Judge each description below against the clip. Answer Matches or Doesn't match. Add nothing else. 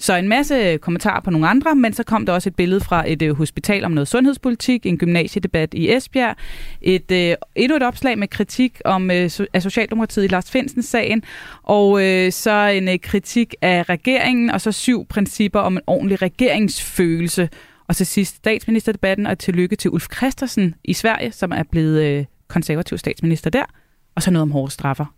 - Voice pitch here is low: Doesn't match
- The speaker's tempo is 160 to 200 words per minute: Matches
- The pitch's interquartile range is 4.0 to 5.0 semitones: Matches